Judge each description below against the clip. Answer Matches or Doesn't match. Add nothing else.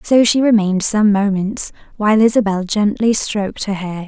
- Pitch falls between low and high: Doesn't match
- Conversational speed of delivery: Matches